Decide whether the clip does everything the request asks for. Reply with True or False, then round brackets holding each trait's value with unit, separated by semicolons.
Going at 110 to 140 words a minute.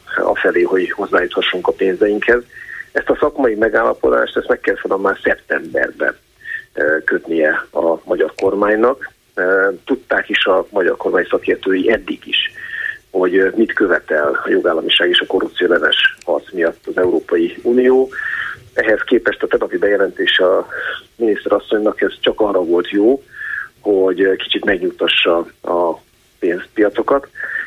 True (130 wpm)